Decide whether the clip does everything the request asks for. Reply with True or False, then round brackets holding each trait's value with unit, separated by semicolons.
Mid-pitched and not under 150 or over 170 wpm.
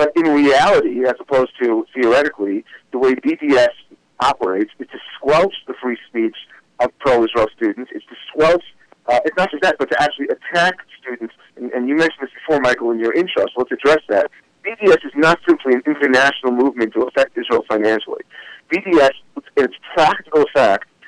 False (155 Hz; 180 wpm)